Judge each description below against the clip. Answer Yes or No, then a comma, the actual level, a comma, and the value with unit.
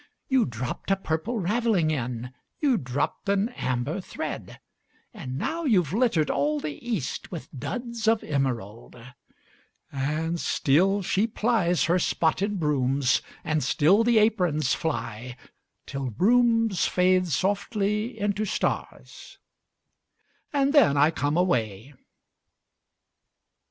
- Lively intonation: Yes, wide, 7.4 semitones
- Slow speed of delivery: Yes, slow, 115 wpm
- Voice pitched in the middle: Yes, medium, 175 Hz